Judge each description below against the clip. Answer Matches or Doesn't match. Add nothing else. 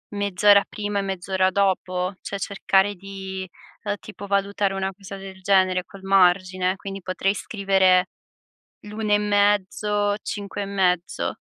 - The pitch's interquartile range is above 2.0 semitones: Doesn't match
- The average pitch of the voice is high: Matches